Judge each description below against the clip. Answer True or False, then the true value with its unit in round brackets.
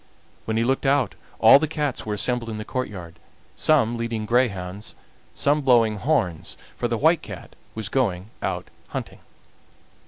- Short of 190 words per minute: True (155 wpm)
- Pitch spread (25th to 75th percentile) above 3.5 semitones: True (4.2 semitones)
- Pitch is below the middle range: True (115 Hz)